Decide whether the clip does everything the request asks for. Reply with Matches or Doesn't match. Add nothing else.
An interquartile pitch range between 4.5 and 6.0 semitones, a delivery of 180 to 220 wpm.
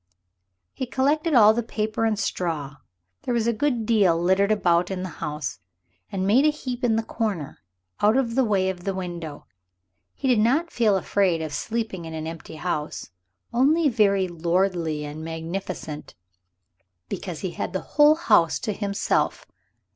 Doesn't match